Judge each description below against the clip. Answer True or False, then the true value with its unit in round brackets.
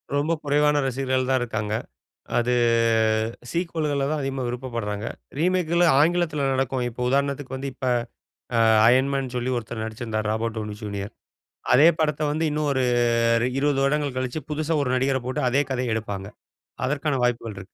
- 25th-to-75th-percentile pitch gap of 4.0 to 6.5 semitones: False (3.6 semitones)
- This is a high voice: False (130 Hz)